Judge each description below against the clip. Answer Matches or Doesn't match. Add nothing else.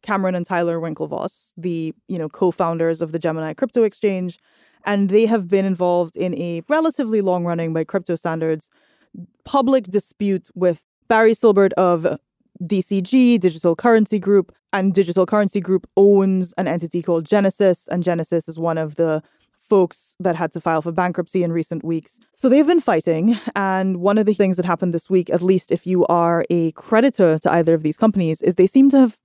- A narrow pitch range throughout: Doesn't match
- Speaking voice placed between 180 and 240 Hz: Matches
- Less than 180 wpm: Doesn't match